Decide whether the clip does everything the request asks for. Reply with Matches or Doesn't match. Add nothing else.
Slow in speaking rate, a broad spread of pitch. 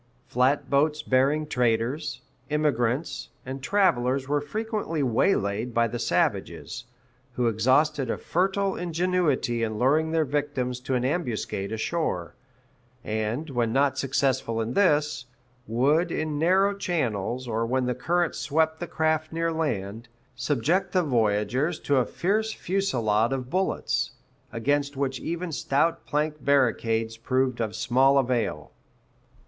Doesn't match